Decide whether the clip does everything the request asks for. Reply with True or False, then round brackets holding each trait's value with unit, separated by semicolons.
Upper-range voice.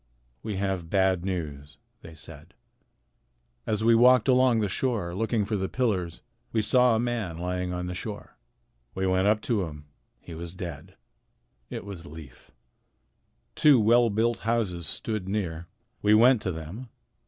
False (100 Hz)